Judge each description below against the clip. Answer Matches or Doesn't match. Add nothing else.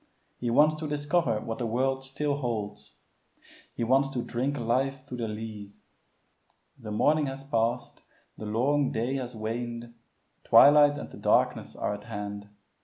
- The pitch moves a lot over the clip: Doesn't match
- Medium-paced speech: Matches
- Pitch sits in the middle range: Doesn't match